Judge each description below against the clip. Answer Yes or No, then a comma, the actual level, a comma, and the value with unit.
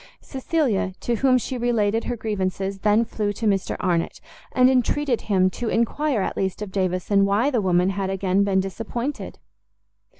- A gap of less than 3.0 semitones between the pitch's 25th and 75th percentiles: No, average, 4.0 semitones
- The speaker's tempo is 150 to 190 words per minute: Yes, average, 165 wpm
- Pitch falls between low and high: No, high, 210 Hz